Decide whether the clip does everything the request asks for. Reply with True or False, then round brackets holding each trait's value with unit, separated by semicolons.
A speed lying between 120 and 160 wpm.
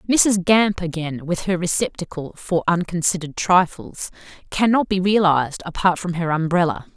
True (140 wpm)